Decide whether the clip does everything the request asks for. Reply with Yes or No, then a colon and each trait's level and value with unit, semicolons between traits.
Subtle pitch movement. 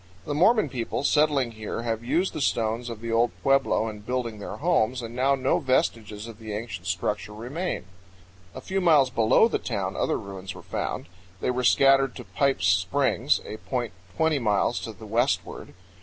No: average, 4.0 semitones